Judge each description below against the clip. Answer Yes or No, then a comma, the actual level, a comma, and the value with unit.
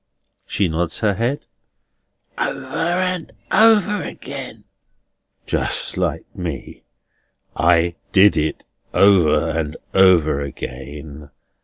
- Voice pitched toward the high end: No, very low, 85 Hz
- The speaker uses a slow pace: Yes, slow, 95 wpm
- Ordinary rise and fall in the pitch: No, wide, 7.4 semitones